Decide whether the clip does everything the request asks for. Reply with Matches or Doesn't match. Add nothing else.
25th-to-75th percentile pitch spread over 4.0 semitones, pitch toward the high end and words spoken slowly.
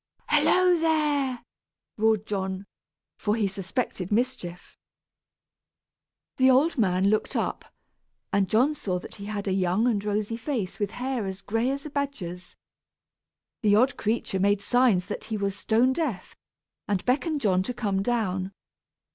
Doesn't match